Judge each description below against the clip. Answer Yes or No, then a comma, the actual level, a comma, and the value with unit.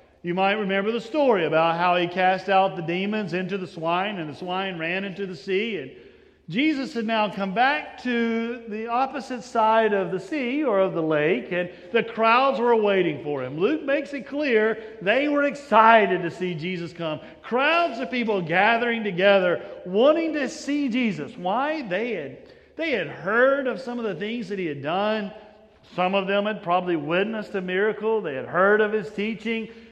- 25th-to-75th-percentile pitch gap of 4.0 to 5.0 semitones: Yes, average, 4.5 semitones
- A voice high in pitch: Yes, high, 215 Hz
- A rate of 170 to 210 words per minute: Yes, average, 190 wpm